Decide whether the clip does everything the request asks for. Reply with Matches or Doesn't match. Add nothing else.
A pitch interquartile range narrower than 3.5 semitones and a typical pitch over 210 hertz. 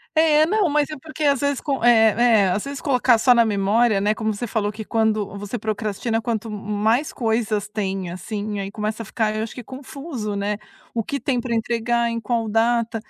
Matches